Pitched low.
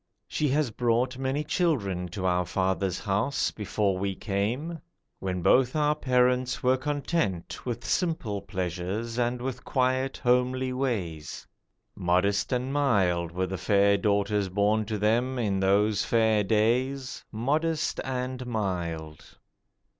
Yes: low, 110 Hz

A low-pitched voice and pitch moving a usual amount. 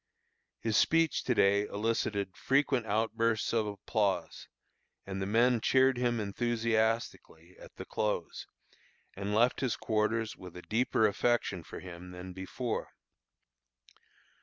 Yes: low, 110 Hz; average, 3.2 semitones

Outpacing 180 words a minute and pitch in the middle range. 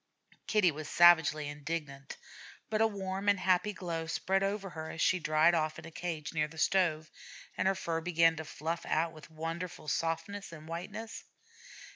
No: average, 175 wpm; medium, 165 Hz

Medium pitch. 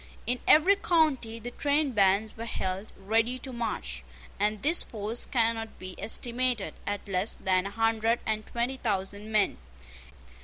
No: high, 225 Hz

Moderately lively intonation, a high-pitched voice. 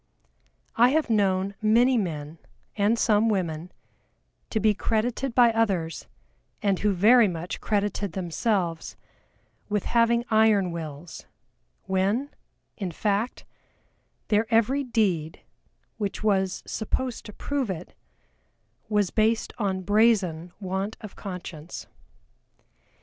Yes: average, 3.6 semitones; high, 205 Hz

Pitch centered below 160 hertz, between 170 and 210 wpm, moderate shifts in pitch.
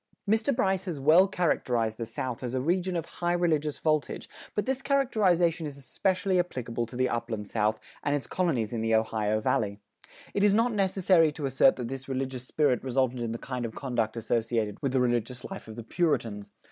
No: low, 135 Hz; average, 195 wpm; wide, 7.1 semitones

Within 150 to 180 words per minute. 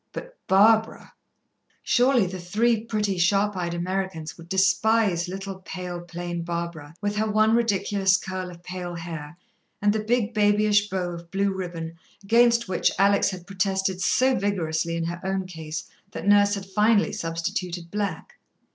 Yes: average, 155 wpm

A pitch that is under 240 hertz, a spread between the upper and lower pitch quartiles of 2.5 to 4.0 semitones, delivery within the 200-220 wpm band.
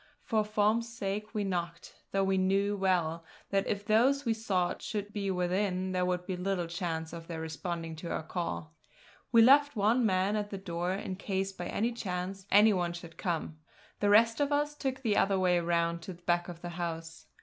Yes: high, 190 Hz; average, 3.4 semitones; fast, 205 wpm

